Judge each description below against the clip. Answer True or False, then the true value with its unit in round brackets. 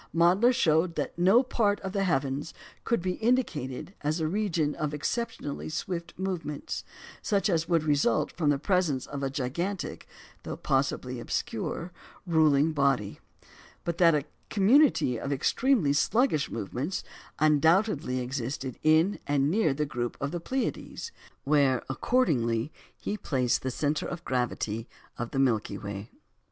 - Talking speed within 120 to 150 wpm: True (145 wpm)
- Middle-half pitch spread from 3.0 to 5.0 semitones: False (5.5 semitones)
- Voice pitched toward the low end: False (155 Hz)